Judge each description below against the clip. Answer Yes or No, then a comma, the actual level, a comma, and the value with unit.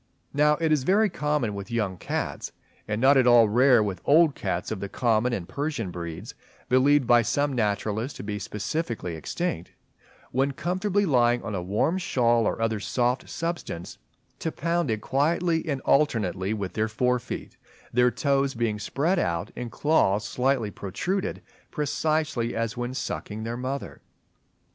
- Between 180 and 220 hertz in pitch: No, low, 120 Hz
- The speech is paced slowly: No, average, 160 wpm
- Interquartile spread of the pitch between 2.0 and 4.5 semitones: No, wide, 5.6 semitones